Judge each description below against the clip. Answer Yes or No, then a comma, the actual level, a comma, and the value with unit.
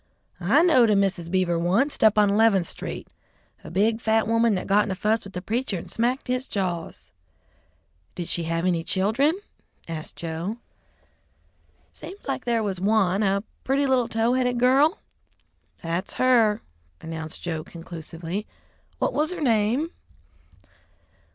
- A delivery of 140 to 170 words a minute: Yes, average, 150 wpm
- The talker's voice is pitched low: No, high, 210 Hz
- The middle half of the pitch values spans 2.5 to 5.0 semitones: No, wide, 5.4 semitones